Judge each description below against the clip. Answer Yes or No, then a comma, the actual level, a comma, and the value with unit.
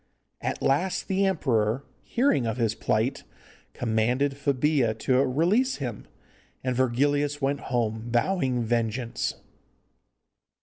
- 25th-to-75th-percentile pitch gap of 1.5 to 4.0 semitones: Yes, average, 3.7 semitones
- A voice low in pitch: Yes, low, 130 Hz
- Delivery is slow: Yes, slow, 105 wpm